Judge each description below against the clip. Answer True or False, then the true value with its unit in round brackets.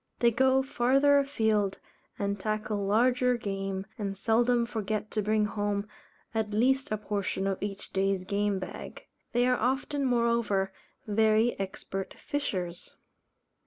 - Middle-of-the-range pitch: False (215 Hz)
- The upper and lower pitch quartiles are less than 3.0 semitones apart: False (3.5 semitones)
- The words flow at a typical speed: False (130 wpm)